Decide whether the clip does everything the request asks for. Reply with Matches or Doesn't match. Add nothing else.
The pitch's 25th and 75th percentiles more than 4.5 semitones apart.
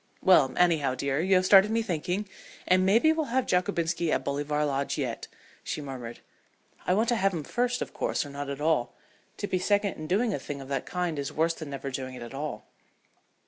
Matches